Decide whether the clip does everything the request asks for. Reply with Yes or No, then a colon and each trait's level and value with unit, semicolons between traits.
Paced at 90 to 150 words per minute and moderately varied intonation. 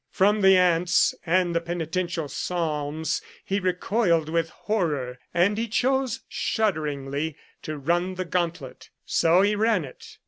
Yes: slow, 135 wpm; average, 3.4 semitones